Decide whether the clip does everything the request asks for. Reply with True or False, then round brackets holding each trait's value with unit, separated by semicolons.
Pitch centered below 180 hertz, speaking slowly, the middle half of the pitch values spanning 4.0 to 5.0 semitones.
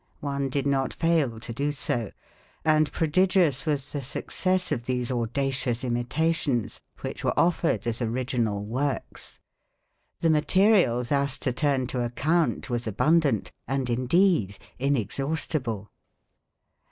True (135 Hz; 120 wpm; 4.4 semitones)